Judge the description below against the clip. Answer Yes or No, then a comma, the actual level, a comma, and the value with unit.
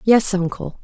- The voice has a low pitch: No, high, 195 Hz